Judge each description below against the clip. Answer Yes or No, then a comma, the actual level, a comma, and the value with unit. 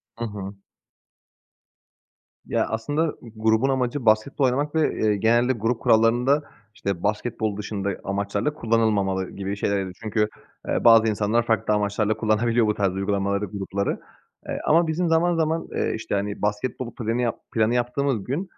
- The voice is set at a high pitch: No, low, 110 Hz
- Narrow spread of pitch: No, average, 3.3 semitones